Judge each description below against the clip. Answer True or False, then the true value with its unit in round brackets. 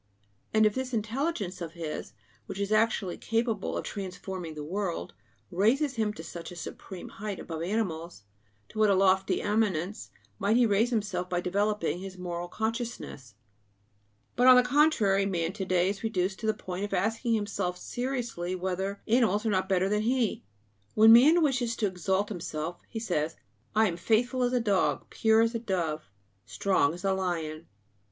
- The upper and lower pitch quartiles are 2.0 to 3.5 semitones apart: False (3.9 semitones)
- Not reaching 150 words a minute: False (175 wpm)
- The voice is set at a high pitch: True (200 Hz)